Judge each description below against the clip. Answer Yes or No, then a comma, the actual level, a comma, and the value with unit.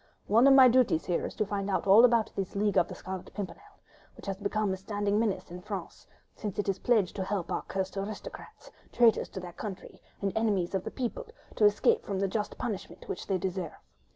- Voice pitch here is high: Yes, high, 200 Hz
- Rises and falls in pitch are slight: Yes, narrow, 2.3 semitones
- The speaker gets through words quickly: Yes, fast, 210 wpm